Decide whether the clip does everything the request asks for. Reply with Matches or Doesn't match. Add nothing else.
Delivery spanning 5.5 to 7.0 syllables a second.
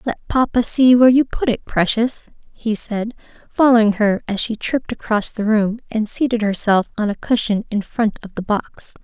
Doesn't match